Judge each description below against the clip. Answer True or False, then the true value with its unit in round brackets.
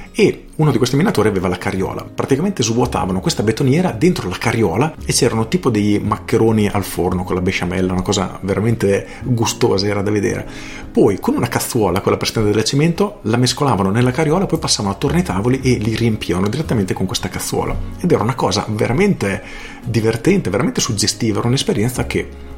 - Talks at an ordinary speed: False (180 wpm)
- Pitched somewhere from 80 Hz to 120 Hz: True (110 Hz)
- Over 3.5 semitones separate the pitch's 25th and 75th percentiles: True (4.6 semitones)